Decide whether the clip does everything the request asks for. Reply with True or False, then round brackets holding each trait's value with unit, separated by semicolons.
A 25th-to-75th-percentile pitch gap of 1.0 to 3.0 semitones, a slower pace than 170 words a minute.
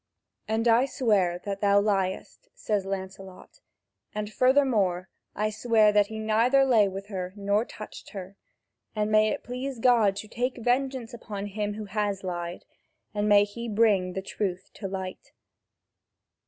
True (2.7 semitones; 155 wpm)